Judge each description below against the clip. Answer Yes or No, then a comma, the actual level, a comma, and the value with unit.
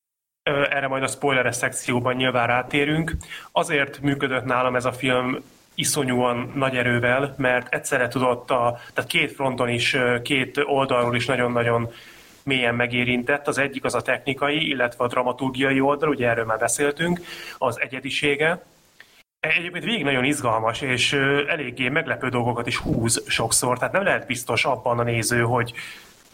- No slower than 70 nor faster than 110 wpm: No, average, 145 wpm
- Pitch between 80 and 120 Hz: No, low, 130 Hz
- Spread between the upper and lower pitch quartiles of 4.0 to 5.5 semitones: No, narrow, 2.6 semitones